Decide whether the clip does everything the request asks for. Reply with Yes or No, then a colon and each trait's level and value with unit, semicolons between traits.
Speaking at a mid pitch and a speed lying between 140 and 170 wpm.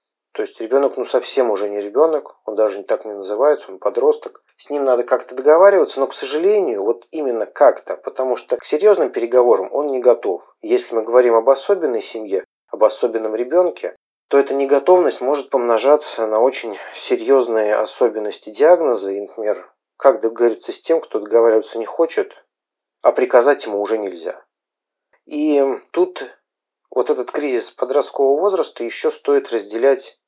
Yes: medium, 165 Hz; average, 155 wpm